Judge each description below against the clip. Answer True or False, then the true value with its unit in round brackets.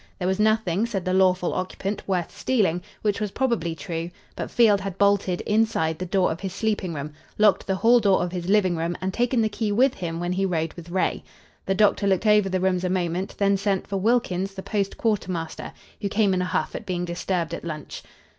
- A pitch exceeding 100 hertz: True (190 Hz)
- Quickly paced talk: True (220 wpm)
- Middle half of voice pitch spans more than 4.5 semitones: False (2.8 semitones)